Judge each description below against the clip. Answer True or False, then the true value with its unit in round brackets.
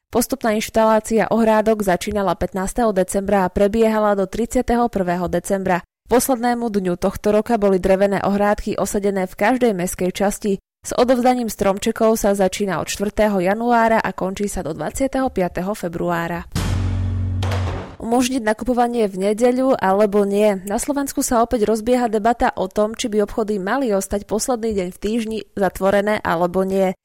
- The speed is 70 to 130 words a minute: False (140 wpm)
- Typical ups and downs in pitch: True (3.2 semitones)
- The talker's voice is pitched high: True (205 Hz)